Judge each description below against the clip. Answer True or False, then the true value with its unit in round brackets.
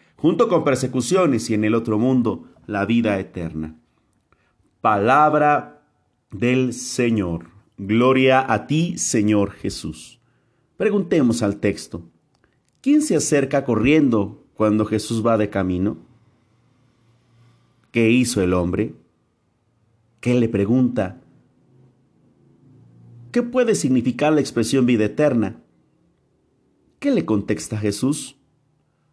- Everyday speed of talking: False (100 wpm)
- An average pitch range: True (3.6 semitones)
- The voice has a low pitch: True (115 Hz)